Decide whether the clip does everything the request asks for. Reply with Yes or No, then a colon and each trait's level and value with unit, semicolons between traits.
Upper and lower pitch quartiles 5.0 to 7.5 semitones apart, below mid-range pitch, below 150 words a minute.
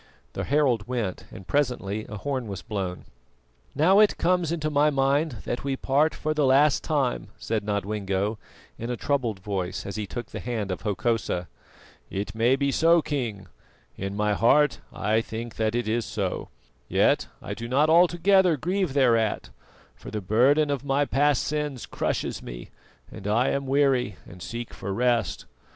No: wide, 5.5 semitones; low, 120 Hz; average, 170 wpm